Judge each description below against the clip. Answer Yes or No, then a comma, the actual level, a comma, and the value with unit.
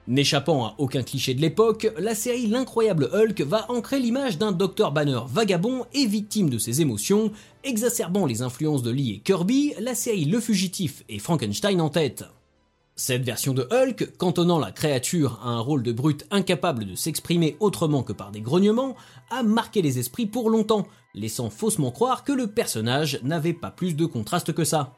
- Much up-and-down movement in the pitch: Yes, wide, 8.3 semitones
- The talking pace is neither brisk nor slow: Yes, average, 185 wpm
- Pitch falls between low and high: Yes, medium, 170 Hz